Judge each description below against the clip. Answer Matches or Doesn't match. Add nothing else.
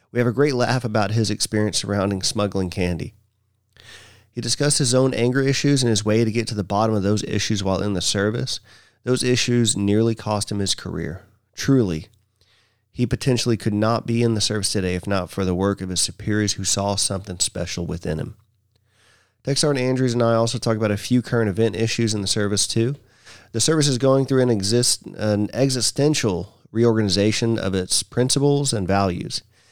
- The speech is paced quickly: Doesn't match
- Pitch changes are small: Doesn't match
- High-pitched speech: Doesn't match